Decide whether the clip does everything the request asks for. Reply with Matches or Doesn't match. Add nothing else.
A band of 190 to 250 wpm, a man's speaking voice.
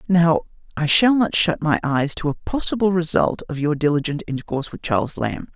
Matches